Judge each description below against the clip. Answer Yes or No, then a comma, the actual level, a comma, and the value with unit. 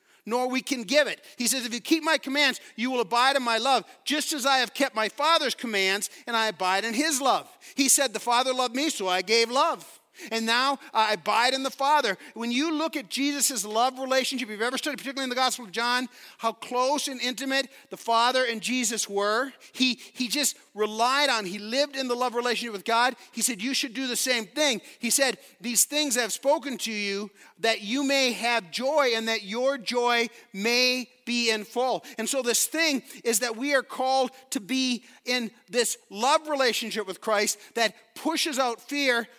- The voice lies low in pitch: No, very high, 250 Hz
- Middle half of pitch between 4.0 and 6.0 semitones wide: No, average, 3.1 semitones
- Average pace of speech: No, fast, 210 wpm